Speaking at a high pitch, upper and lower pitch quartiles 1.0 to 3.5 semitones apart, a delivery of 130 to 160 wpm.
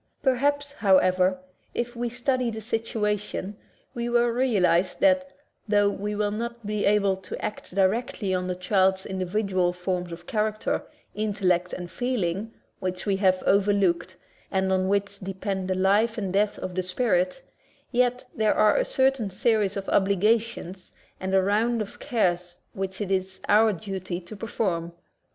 Yes: high, 200 Hz; average, 3.2 semitones; average, 155 wpm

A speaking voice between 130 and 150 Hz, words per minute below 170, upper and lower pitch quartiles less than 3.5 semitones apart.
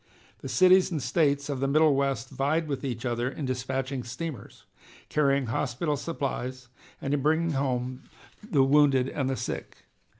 Yes: low, 135 Hz; average, 155 wpm; narrow, 2.6 semitones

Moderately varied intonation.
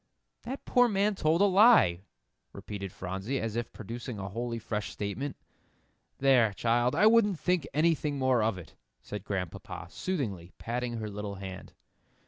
No: wide, 7.5 semitones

